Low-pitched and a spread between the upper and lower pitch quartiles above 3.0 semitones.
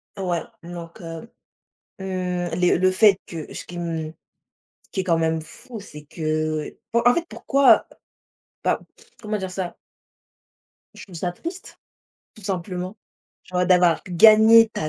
No: medium, 180 Hz; average, 3.6 semitones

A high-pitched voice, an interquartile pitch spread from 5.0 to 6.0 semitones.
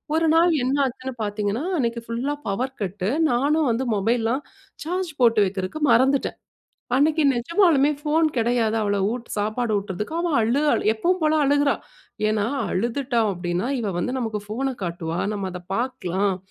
Yes: high, 235 Hz; wide, 5.5 semitones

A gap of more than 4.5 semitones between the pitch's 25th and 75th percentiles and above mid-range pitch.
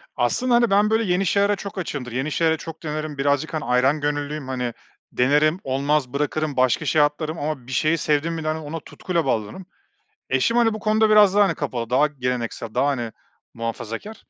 No: average, 5.2 semitones; medium, 150 Hz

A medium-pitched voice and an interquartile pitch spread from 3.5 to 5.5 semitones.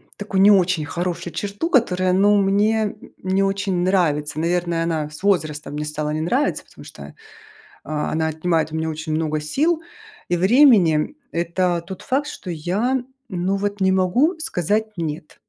Yes: medium, 180 Hz; average, 4.3 semitones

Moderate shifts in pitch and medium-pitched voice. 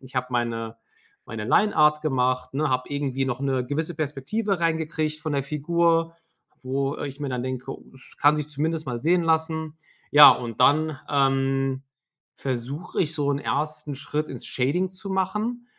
Yes: average, 3.3 semitones; medium, 145 Hz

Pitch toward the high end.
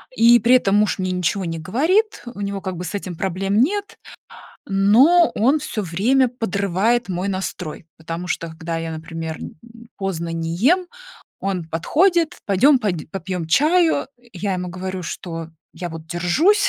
Yes: high, 195 Hz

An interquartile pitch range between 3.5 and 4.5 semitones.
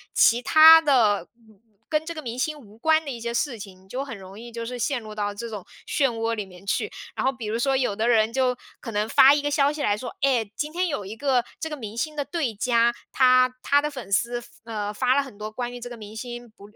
Yes: average, 4.2 semitones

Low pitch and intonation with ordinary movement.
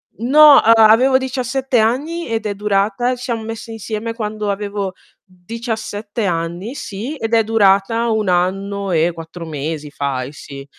No: high, 215 Hz; average, 3.8 semitones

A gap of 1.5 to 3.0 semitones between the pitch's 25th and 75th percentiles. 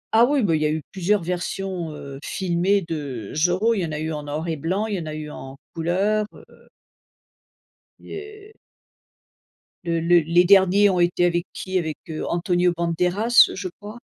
No: average, 3.6 semitones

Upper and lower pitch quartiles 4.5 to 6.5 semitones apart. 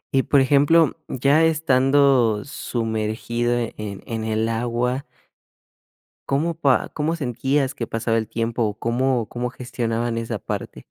No: average, 3.4 semitones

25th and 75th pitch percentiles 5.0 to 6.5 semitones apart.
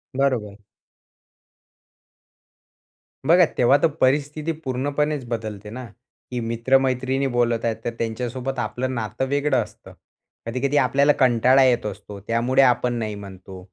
No: average, 2.9 semitones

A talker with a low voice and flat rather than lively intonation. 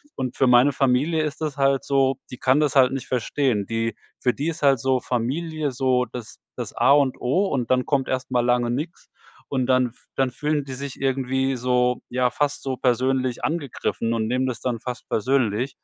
Yes: low, 130 Hz; narrow, 1.9 semitones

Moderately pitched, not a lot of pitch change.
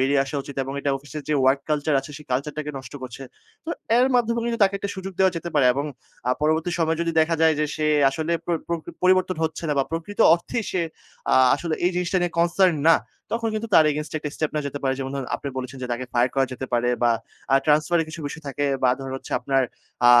No: medium, 155 Hz; average, 4.1 semitones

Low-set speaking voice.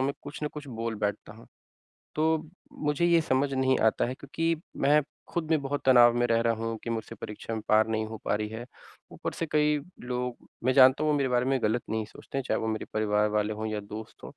Yes: low, 120 Hz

